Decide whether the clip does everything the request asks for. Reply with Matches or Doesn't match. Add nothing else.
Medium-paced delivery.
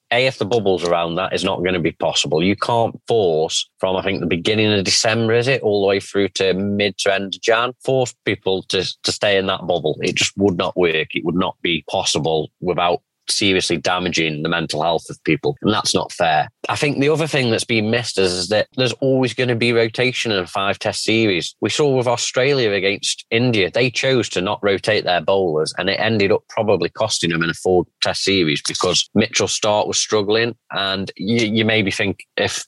Doesn't match